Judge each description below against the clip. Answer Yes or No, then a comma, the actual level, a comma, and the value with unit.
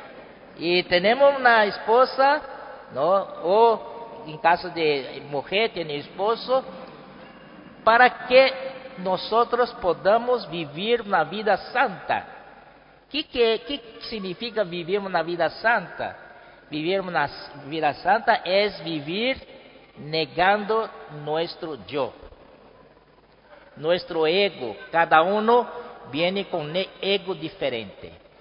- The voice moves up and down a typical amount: No, wide, 6.2 semitones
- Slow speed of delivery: Yes, slow, 95 wpm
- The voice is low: No, high, 195 Hz